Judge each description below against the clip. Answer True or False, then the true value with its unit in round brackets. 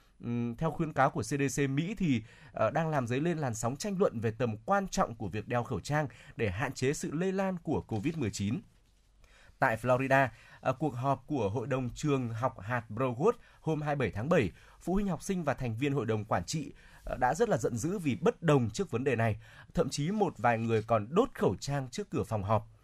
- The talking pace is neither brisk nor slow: True (220 wpm)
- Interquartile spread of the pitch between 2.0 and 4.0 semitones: False (4.8 semitones)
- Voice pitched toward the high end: False (135 Hz)